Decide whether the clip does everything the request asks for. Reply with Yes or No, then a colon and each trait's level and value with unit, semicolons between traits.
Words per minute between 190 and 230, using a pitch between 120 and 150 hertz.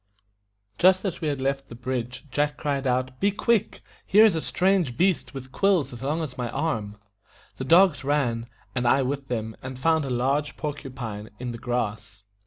Yes: average, 195 wpm; low, 135 Hz